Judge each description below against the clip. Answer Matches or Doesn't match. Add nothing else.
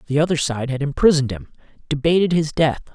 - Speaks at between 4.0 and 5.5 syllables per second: Doesn't match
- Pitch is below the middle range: Doesn't match